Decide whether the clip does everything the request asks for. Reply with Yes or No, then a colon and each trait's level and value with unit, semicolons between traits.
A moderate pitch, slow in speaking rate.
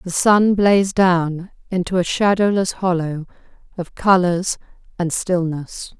Yes: medium, 180 Hz; slow, 120 wpm